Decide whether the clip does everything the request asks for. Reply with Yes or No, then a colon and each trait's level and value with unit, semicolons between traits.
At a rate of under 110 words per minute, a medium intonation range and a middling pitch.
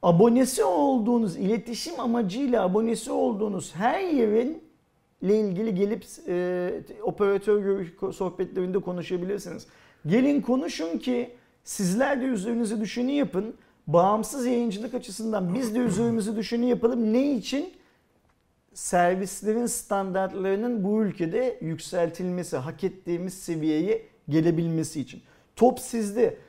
No: average, 100 wpm; average, 4.5 semitones; high, 220 Hz